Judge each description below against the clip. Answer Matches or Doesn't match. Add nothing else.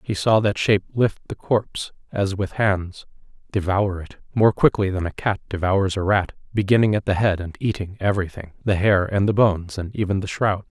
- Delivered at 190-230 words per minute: Matches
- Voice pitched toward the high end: Doesn't match